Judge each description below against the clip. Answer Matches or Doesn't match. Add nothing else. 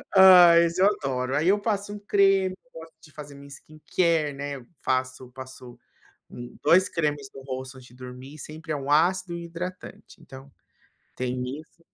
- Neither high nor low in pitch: Matches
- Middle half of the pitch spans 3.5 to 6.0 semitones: Matches